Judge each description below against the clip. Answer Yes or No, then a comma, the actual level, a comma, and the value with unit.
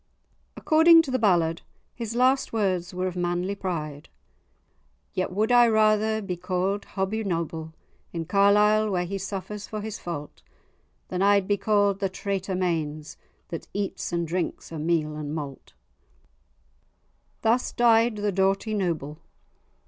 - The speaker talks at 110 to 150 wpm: Yes, average, 140 wpm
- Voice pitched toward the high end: Yes, high, 195 Hz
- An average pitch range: Yes, average, 3.7 semitones